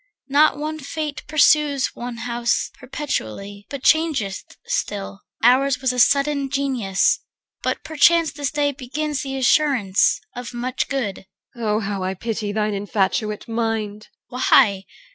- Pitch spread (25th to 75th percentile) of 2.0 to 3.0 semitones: No, average, 5.3 semitones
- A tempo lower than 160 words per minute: Yes, average, 140 wpm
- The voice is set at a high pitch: Yes, very high, 250 Hz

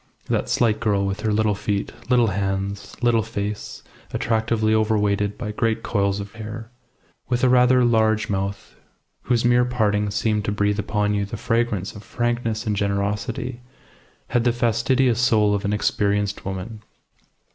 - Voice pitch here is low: Yes, low, 110 Hz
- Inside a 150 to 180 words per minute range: Yes, average, 155 wpm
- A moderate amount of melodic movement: No, narrow, 2.3 semitones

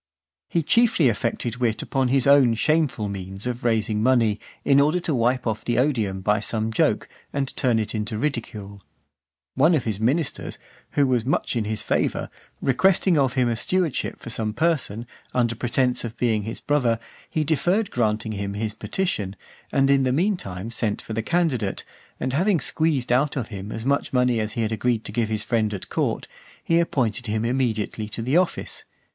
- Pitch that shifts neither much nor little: Yes, average, 4.3 semitones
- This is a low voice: Yes, low, 120 Hz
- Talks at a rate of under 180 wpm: No, average, 190 wpm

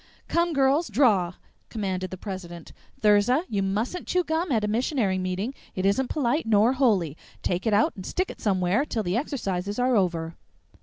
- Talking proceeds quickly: No, average, 175 wpm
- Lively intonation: Yes, wide, 5.9 semitones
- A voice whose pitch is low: No, high, 210 Hz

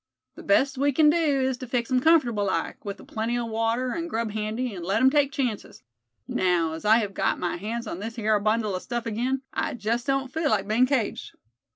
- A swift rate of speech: Yes, fast, 230 wpm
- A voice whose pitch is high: Yes, high, 235 Hz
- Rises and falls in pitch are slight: No, average, 3.7 semitones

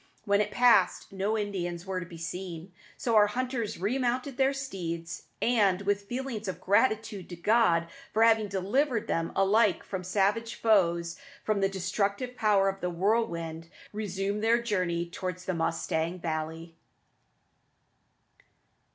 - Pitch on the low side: No, high, 200 Hz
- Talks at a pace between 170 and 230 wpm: No, average, 145 wpm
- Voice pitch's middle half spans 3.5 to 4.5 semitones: Yes, average, 4.2 semitones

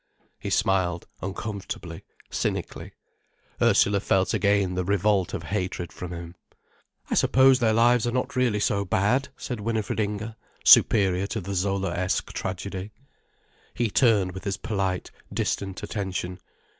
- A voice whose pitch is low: Yes, low, 100 Hz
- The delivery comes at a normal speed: No, slow, 130 wpm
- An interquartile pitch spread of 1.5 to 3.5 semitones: Yes, average, 2.8 semitones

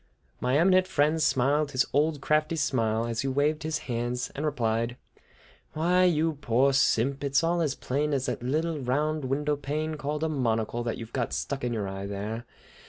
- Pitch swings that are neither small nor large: Yes, average, 4.0 semitones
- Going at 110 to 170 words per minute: No, average, 185 wpm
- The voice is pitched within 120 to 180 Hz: Yes, medium, 140 Hz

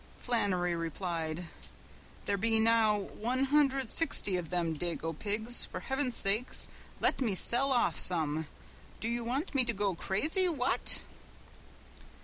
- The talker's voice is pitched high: Yes, high, 220 Hz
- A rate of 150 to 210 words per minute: No, slow, 135 wpm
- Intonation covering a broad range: Yes, wide, 6.1 semitones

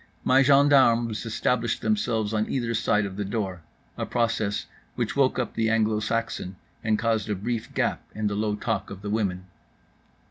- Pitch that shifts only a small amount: Yes, narrow, 2.0 semitones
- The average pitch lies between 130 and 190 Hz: No, low, 110 Hz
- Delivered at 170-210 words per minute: Yes, average, 175 wpm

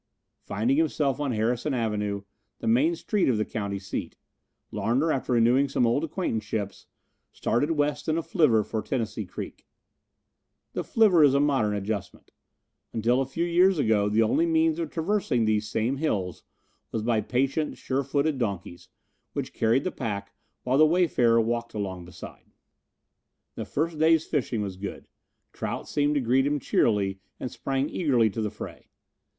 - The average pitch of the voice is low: Yes, low, 125 Hz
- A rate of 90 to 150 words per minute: No, average, 160 wpm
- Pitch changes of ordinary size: No, wide, 5.7 semitones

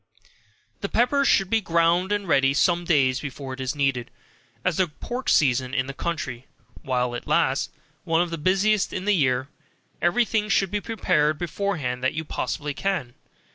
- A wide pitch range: Yes, wide, 6.5 semitones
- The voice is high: No, medium, 165 Hz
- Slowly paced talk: No, average, 180 wpm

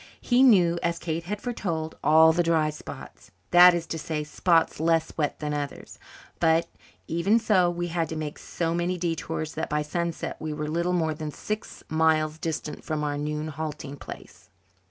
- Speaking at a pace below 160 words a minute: No, average, 180 wpm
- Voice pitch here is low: No, medium, 160 Hz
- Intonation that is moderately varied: No, narrow, 2.0 semitones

